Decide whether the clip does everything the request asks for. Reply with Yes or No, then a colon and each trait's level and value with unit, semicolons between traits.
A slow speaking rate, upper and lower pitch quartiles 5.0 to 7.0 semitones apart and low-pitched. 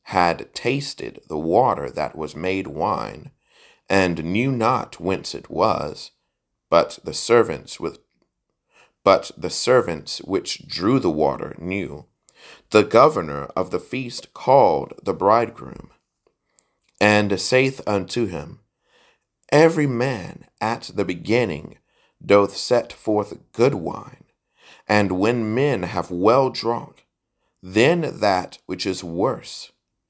Yes: slow, 120 wpm; average, 5.3 semitones; low, 100 Hz